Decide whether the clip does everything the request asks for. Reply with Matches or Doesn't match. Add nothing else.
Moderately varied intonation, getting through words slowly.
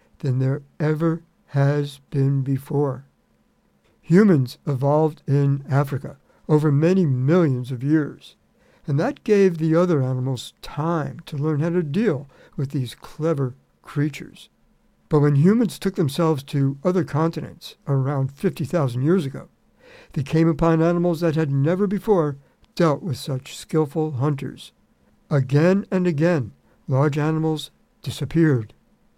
Matches